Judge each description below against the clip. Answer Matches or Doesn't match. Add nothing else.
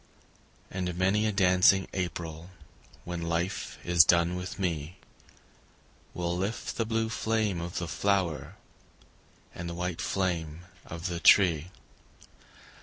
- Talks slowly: Matches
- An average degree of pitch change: Doesn't match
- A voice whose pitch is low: Matches